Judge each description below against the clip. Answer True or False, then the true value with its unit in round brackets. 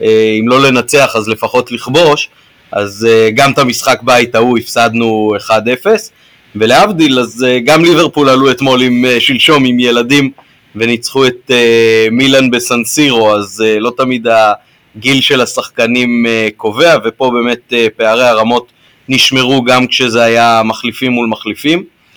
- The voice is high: False (120 Hz)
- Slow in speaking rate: False (125 wpm)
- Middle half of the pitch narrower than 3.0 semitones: True (2.6 semitones)